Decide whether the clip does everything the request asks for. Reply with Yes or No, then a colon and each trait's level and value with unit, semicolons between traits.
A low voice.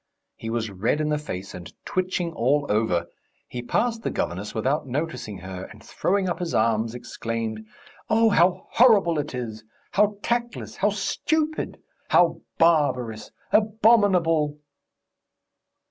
No: medium, 150 Hz